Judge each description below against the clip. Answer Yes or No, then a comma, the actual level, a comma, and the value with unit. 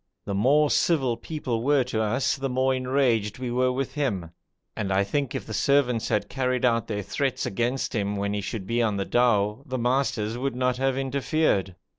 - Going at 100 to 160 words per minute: No, average, 200 wpm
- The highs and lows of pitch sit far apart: No, average, 4.1 semitones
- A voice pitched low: Yes, low, 125 Hz